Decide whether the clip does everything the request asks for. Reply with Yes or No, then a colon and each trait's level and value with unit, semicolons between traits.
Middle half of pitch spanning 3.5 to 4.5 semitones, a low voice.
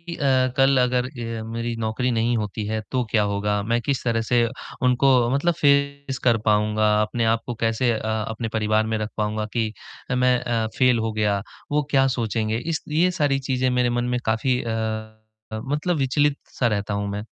No: average, 2.8 semitones; low, 115 Hz